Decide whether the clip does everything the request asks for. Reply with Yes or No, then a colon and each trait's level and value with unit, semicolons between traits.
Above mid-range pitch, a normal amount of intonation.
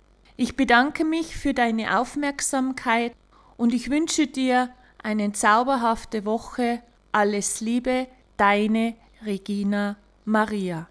Yes: high, 235 Hz; average, 3.4 semitones